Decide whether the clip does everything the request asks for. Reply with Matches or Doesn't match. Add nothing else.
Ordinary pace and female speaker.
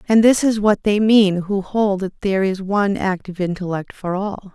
Doesn't match